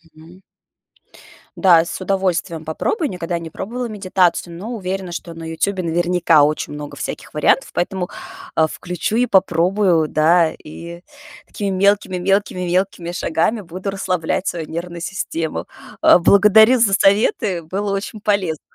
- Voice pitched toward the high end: No, medium, 180 Hz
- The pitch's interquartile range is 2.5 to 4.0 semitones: Yes, average, 2.8 semitones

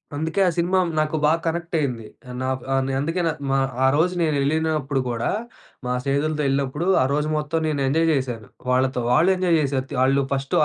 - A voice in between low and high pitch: Yes, medium, 145 Hz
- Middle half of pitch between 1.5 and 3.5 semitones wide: Yes, average, 3.2 semitones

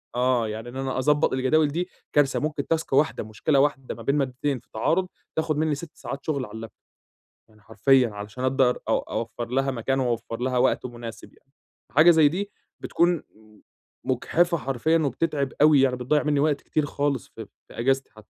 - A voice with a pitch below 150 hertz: Yes, low, 135 Hz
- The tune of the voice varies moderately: Yes, average, 3.6 semitones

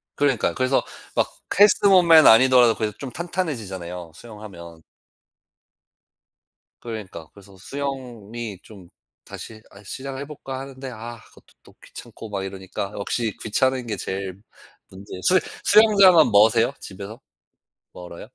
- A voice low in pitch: Yes, low, 115 Hz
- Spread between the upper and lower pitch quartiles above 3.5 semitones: Yes, wide, 5.4 semitones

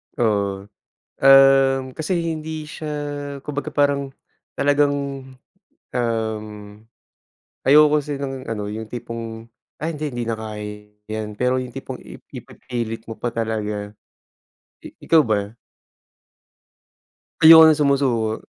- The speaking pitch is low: Yes, low, 125 Hz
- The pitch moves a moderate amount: Yes, average, 4.5 semitones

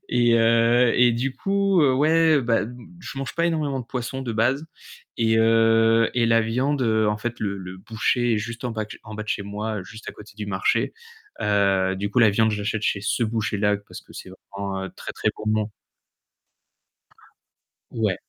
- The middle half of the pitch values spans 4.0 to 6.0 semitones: No, average, 2.8 semitones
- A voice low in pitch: Yes, low, 115 Hz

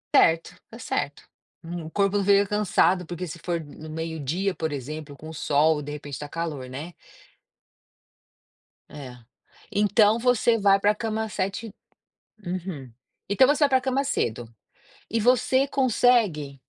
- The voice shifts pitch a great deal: Yes, wide, 6.0 semitones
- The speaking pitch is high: No, medium, 180 Hz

